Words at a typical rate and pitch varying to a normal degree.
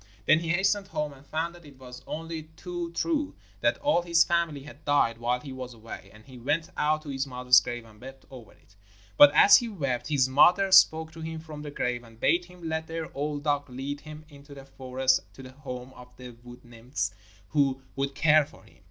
No: fast, 220 wpm; average, 4.0 semitones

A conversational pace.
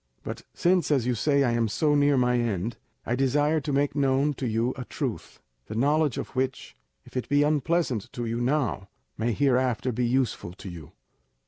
Yes: average, 195 wpm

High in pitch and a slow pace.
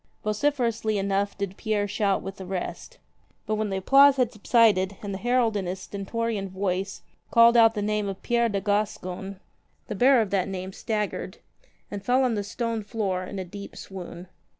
No: high, 205 Hz; average, 190 wpm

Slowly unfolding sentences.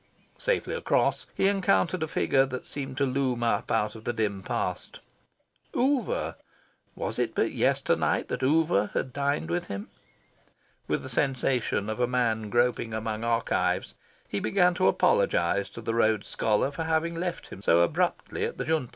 No: average, 165 wpm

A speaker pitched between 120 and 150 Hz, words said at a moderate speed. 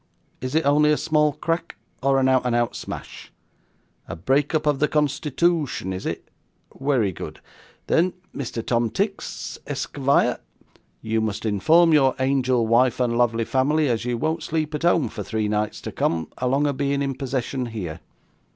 Yes: low, 135 Hz; average, 175 wpm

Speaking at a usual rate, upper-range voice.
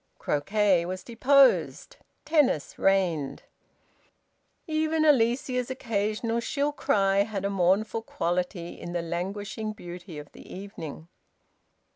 No: slow, 105 wpm; high, 200 Hz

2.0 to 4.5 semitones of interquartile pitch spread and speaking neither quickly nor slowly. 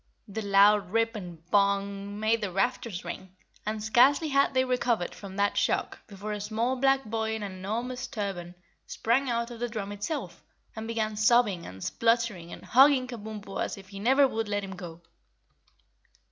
Yes: average, 3.2 semitones; average, 175 wpm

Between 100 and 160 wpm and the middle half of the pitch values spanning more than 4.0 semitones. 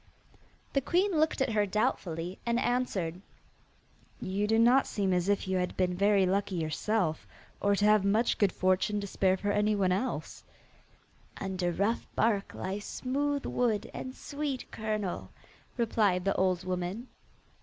No: average, 150 wpm; average, 3.7 semitones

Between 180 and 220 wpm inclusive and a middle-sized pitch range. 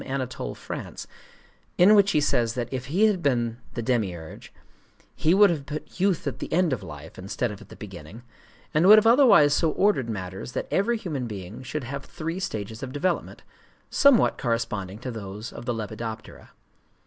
No: average, 185 wpm; wide, 7.5 semitones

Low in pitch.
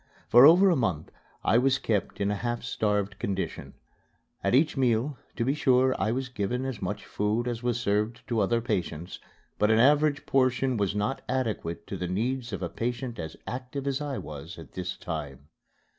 Yes: low, 120 Hz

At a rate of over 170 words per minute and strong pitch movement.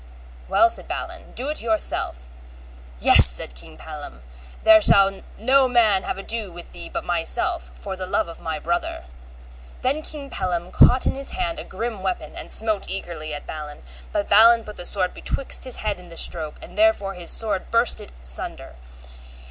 Yes: average, 180 wpm; wide, 6.3 semitones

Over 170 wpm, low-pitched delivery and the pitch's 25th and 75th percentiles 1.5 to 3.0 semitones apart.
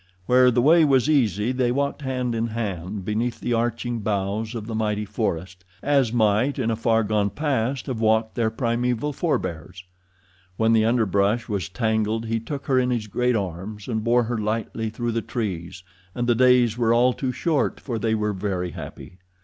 Yes: average, 190 wpm; low, 115 Hz; average, 2.7 semitones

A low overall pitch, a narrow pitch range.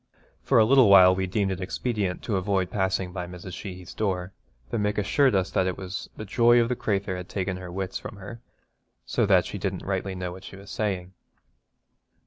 Yes: very low, 95 Hz; narrow, 2.1 semitones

